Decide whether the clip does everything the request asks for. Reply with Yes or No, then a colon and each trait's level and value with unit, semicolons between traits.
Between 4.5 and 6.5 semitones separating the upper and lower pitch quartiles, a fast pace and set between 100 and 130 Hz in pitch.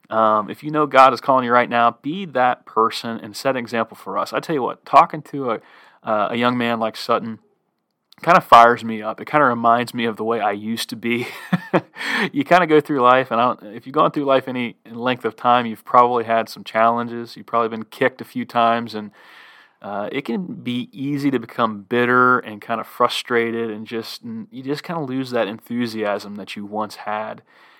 No: narrow, 2.6 semitones; fast, 230 wpm; low, 120 Hz